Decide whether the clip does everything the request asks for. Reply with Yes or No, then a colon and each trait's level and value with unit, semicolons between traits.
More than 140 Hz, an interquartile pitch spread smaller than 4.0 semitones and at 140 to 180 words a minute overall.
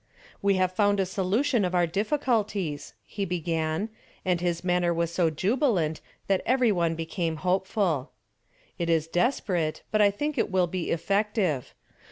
Yes: medium, 185 Hz; average, 3.5 semitones; average, 155 wpm